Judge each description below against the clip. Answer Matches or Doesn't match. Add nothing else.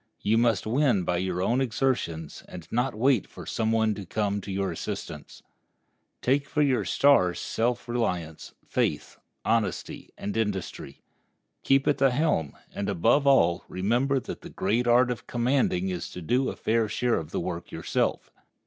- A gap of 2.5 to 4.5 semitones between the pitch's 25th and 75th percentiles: Doesn't match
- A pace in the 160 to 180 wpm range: Matches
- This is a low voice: Matches